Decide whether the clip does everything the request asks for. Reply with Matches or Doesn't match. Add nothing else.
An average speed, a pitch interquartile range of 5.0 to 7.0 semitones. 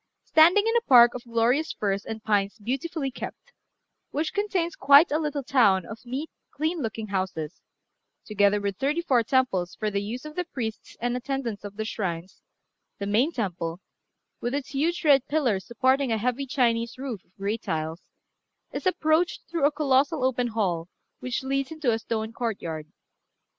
Matches